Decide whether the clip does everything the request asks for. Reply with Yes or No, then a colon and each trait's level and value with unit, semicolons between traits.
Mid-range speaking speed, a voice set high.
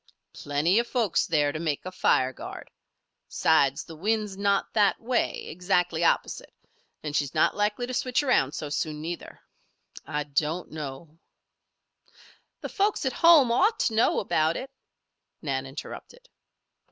No: average, 145 wpm; medium, 170 Hz